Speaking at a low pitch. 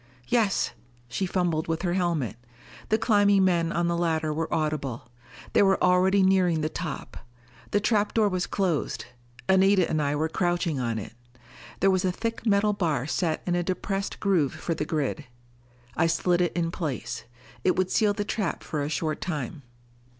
No: medium, 175 Hz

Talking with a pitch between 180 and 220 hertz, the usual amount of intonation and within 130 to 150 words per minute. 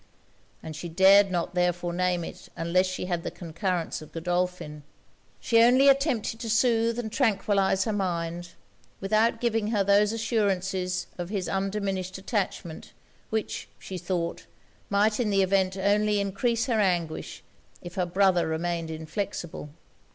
Yes: high, 190 Hz; average, 3.3 semitones; average, 145 wpm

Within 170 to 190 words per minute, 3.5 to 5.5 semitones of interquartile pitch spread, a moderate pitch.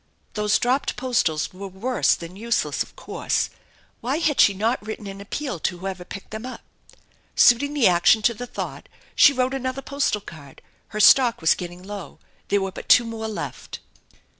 No: average, 180 wpm; average, 4.8 semitones; high, 220 Hz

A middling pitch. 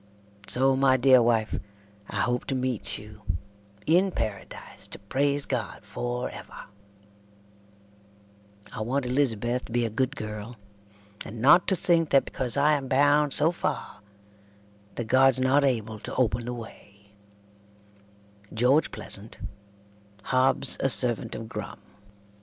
No: low, 125 Hz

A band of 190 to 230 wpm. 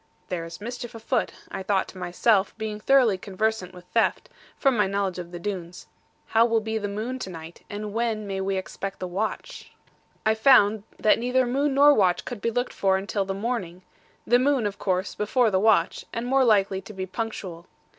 Yes: average, 200 wpm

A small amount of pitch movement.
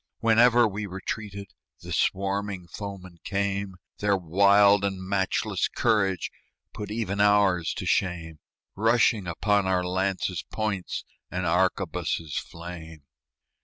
Yes: narrow, 2.1 semitones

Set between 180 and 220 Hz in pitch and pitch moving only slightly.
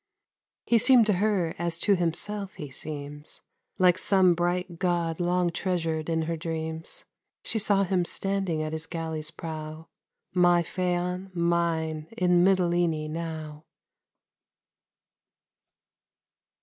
No: medium, 170 Hz; narrow, 2.3 semitones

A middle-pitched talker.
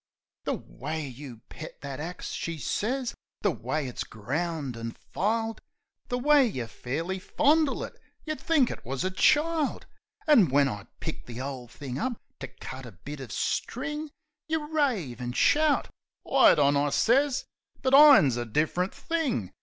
Yes: medium, 165 Hz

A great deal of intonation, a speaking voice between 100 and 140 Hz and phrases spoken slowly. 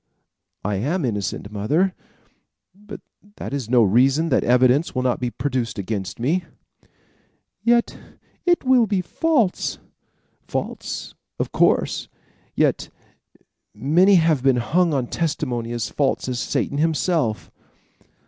Yes: wide, 6.7 semitones; low, 135 Hz; slow, 120 wpm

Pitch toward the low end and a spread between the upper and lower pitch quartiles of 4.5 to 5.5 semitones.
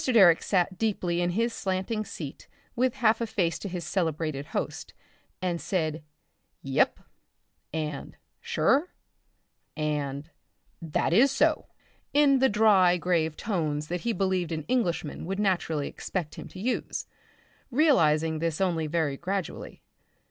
No: medium, 175 Hz; average, 5.1 semitones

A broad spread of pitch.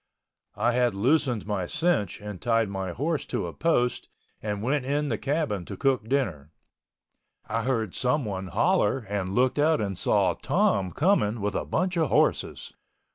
Yes: wide, 5.9 semitones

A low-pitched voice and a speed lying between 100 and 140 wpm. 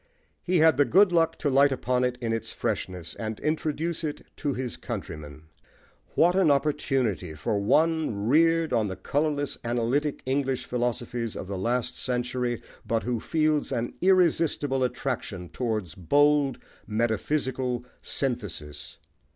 Yes: low, 125 Hz; slow, 135 wpm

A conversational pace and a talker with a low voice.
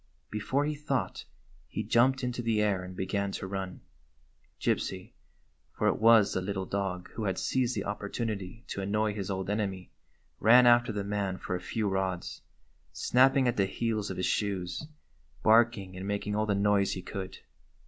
Yes: average, 185 wpm; low, 100 Hz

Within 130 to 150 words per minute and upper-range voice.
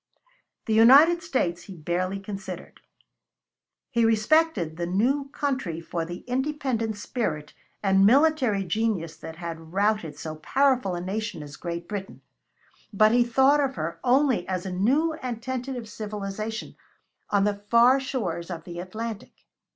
Yes: average, 145 wpm; high, 210 Hz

